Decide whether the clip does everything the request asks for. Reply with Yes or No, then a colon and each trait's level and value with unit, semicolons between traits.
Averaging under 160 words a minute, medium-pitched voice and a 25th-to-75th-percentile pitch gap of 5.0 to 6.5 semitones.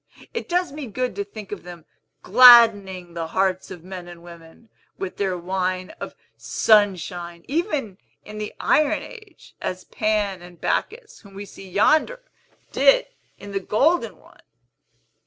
No: average, 150 wpm; high, 200 Hz; wide, 5.6 semitones